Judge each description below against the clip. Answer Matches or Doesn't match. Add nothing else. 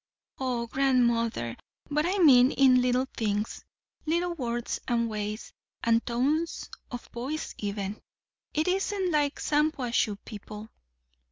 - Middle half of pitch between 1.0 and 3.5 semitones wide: Doesn't match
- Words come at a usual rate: Doesn't match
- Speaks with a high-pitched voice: Matches